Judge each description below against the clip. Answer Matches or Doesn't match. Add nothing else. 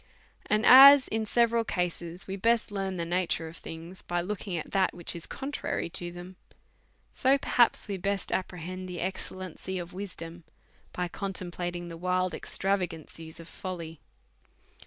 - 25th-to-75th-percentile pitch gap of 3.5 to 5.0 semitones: Doesn't match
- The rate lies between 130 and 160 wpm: Matches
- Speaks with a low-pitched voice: Doesn't match